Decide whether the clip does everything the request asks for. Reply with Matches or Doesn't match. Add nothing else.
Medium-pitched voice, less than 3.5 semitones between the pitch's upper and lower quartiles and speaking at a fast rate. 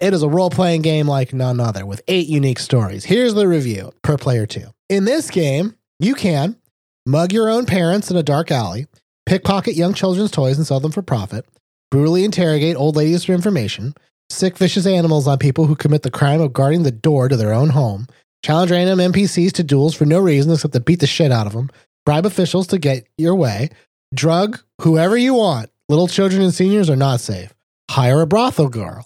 Doesn't match